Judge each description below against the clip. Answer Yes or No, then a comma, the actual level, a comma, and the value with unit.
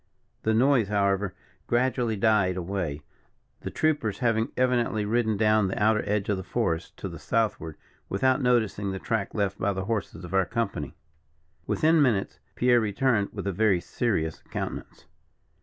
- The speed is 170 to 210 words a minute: No, average, 160 wpm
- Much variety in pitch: No, average, 3.5 semitones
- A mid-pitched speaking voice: No, low, 105 Hz